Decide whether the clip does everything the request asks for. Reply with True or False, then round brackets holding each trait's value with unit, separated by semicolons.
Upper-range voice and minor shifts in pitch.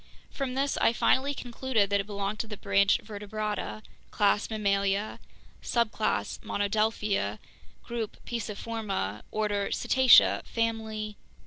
True (215 Hz; 2.1 semitones)